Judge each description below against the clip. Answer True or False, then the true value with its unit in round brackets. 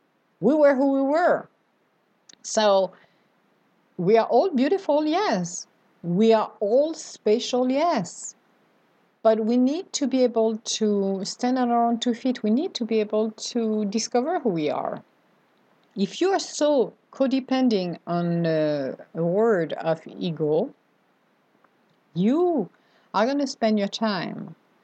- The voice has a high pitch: True (225 Hz)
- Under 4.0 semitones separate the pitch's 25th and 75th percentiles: False (4.8 semitones)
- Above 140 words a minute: False (135 wpm)